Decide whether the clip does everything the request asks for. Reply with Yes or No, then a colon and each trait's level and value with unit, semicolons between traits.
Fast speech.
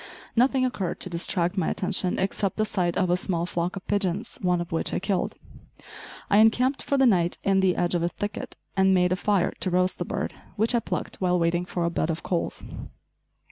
Yes: fast, 220 wpm